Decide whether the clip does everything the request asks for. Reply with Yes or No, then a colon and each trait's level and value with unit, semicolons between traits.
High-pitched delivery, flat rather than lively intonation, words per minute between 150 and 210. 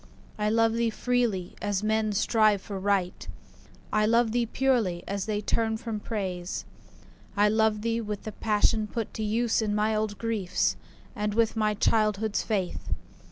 Yes: high, 215 Hz; narrow, 1.6 semitones; average, 160 wpm